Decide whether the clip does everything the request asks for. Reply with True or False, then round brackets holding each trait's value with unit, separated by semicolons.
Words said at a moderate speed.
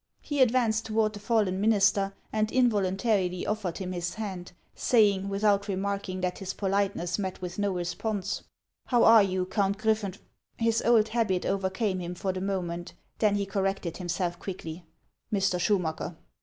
True (175 wpm)